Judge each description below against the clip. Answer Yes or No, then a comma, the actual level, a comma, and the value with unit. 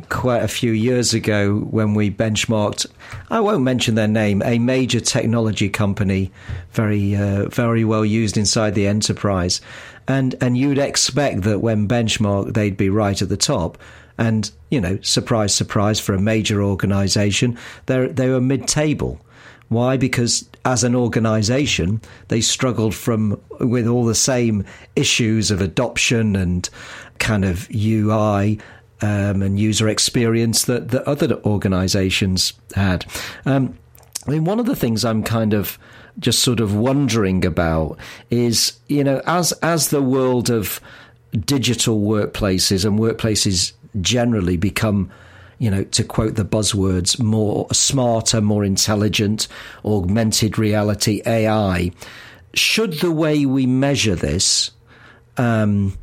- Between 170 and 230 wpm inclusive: No, average, 140 wpm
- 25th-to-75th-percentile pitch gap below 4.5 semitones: Yes, average, 3.1 semitones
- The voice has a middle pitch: No, low, 110 Hz